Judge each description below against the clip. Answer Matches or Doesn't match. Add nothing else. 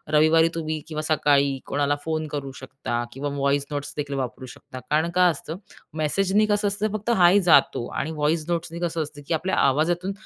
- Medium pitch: Matches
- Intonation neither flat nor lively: Matches